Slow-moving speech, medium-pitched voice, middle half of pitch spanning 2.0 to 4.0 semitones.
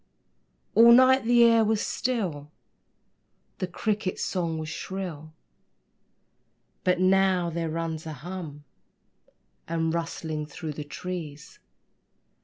Yes: slow, 105 wpm; medium, 170 Hz; average, 3.5 semitones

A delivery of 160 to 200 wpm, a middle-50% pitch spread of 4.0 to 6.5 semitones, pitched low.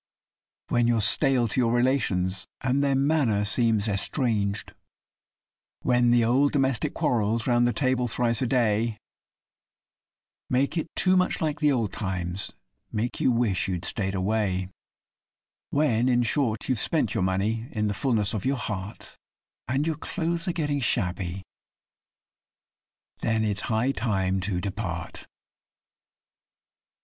No: slow, 135 wpm; average, 4.4 semitones; low, 115 Hz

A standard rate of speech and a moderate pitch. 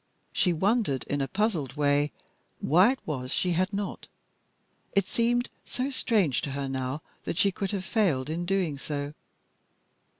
Yes: average, 165 wpm; medium, 175 Hz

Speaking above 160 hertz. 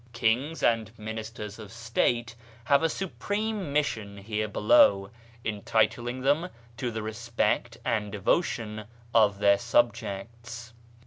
No: low, 115 Hz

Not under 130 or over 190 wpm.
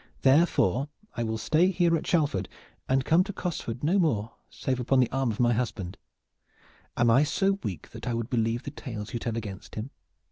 No: average, 200 wpm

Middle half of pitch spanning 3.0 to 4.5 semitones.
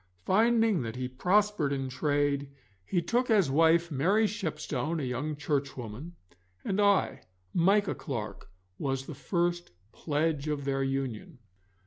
No: wide, 5.4 semitones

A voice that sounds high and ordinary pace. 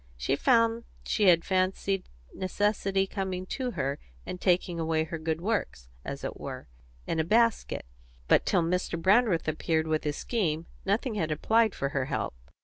No: medium, 180 Hz; average, 165 wpm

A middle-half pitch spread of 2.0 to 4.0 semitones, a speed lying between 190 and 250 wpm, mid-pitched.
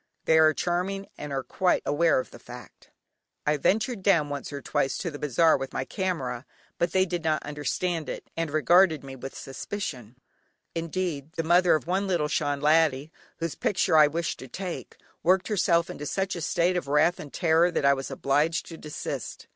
Yes: average, 3.6 semitones; average, 195 wpm; medium, 160 Hz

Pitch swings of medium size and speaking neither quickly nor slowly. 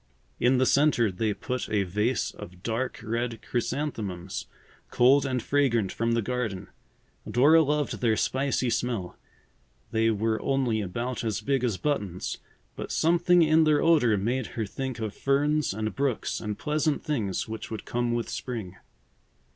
Yes: average, 4.1 semitones; average, 155 wpm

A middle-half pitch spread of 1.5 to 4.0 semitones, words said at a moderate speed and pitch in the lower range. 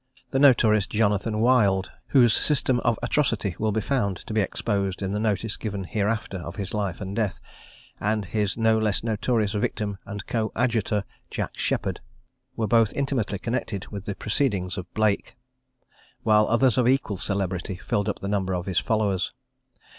Yes: narrow, 2.4 semitones; average, 165 wpm; low, 105 Hz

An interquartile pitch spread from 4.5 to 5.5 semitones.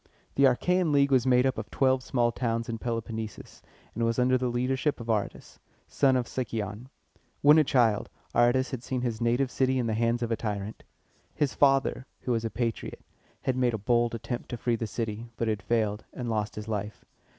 No: narrow, 2.4 semitones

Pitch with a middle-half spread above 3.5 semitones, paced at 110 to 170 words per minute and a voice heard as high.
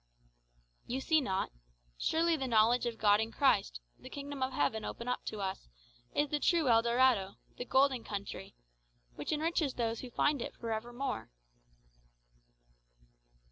Yes: average, 4.2 semitones; average, 155 wpm; high, 245 Hz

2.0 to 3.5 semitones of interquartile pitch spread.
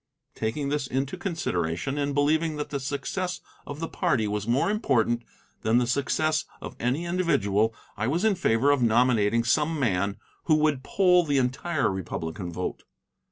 No: wide, 5.6 semitones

